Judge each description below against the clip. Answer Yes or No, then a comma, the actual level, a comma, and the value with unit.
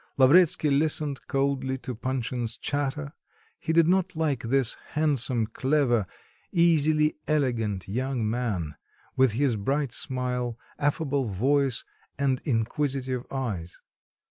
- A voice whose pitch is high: No, low, 135 Hz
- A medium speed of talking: No, slow, 110 wpm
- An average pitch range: Yes, average, 3.3 semitones